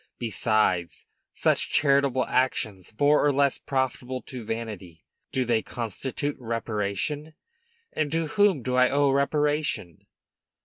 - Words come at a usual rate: No, slow, 120 wpm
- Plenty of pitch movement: No, average, 4.4 semitones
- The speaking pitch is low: Yes, low, 130 Hz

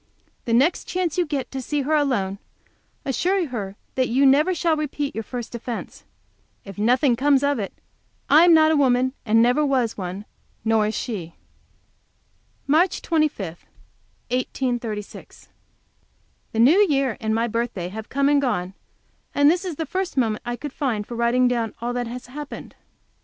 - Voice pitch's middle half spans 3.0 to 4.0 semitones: No, average, 4.6 semitones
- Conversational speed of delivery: Yes, average, 170 wpm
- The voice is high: Yes, very high, 255 Hz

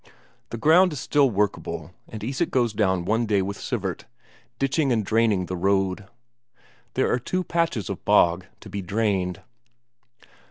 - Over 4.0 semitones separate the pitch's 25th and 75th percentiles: Yes, average, 4.9 semitones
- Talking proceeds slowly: No, average, 155 wpm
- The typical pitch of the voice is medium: No, low, 105 Hz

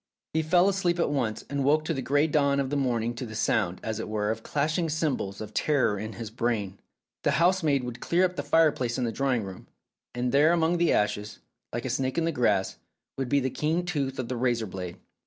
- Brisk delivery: Yes, fast, 230 wpm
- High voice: No, low, 135 Hz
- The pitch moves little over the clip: No, wide, 5.5 semitones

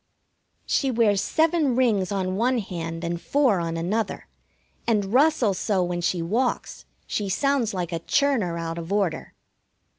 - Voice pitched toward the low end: No, high, 200 Hz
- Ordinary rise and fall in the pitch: No, wide, 6.3 semitones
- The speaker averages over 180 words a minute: No, average, 150 wpm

